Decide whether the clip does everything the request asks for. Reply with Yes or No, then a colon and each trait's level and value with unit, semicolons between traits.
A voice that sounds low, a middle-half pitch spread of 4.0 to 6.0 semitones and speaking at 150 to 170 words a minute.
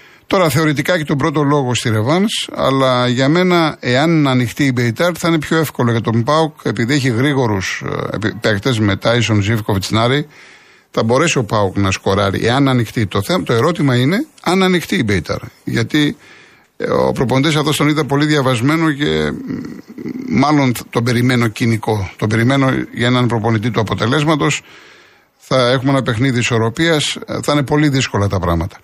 Yes: low, 130 Hz; average, 4.7 semitones; average, 165 wpm